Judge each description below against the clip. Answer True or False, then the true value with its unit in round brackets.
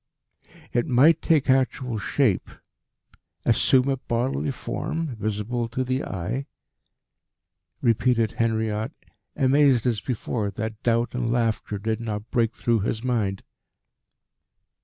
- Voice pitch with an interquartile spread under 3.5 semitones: True (2.8 semitones)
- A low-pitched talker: True (120 Hz)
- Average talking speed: False (115 wpm)